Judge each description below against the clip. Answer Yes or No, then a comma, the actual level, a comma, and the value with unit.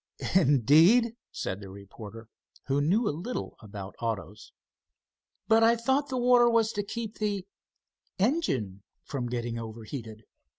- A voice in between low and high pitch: Yes, medium, 145 Hz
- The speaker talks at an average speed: No, slow, 130 wpm